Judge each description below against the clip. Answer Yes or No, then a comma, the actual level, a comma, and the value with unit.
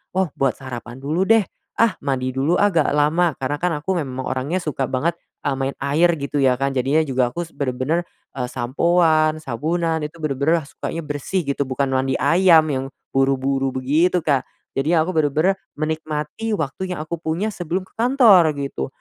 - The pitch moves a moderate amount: Yes, average, 4.1 semitones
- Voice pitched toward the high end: No, medium, 150 Hz